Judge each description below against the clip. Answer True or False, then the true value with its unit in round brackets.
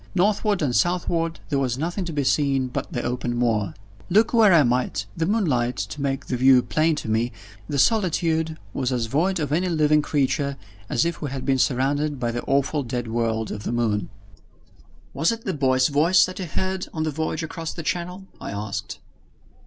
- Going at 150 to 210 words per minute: True (200 wpm)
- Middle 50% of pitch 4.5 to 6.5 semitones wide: True (5.2 semitones)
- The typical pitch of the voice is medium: True (145 Hz)